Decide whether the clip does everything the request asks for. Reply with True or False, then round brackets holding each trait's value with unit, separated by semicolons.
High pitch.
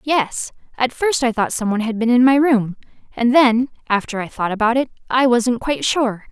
True (240 Hz)